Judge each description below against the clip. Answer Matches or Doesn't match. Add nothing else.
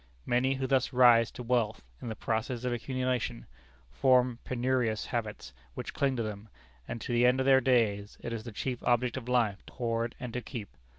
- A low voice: Matches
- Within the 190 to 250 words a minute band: Matches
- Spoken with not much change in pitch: Matches